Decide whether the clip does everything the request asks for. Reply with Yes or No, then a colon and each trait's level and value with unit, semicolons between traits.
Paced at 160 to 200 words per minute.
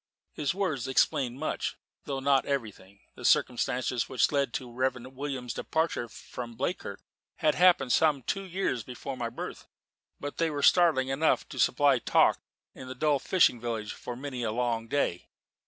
Yes: average, 170 wpm